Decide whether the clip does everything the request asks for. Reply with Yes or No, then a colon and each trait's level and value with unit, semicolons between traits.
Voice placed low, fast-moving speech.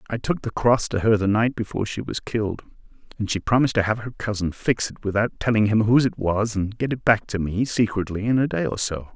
Yes: low, 110 Hz; fast, 255 wpm